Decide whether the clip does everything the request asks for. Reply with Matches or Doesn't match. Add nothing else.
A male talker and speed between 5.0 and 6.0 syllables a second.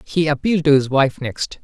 Matches